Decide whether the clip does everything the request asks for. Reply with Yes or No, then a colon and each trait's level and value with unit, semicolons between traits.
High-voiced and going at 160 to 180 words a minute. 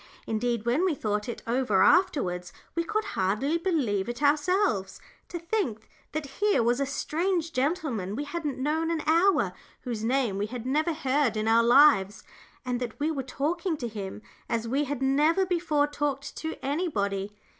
Yes: very high, 275 Hz; average, 170 wpm